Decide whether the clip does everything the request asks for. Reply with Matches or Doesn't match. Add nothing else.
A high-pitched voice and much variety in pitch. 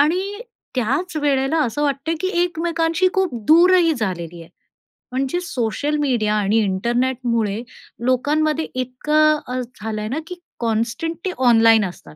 Matches